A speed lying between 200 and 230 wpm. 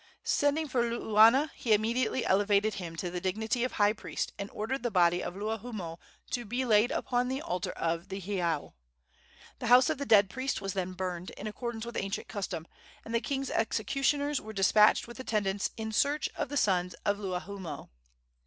No: average, 185 wpm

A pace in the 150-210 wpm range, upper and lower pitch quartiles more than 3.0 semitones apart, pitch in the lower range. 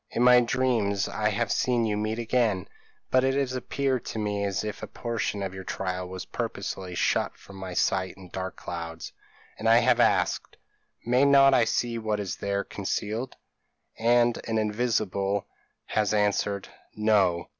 Yes: average, 165 wpm; average, 3.5 semitones; low, 105 Hz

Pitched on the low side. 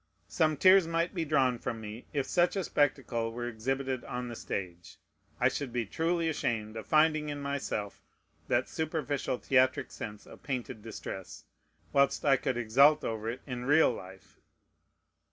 Yes: low, 130 Hz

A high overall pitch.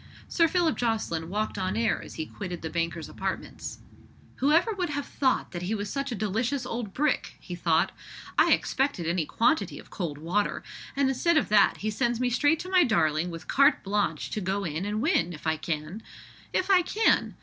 Yes: high, 215 Hz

